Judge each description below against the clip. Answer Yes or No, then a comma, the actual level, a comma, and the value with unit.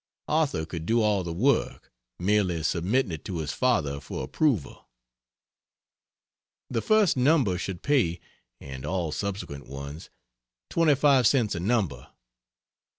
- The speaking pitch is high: No, very low, 95 Hz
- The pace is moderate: No, slow, 125 wpm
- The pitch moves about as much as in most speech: No, wide, 7.9 semitones